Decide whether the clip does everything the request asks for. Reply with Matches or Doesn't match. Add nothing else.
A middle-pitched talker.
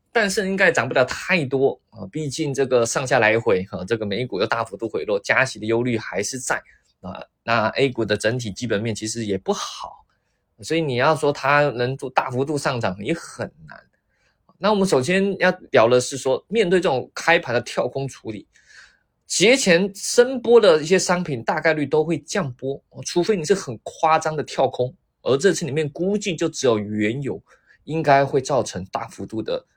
Matches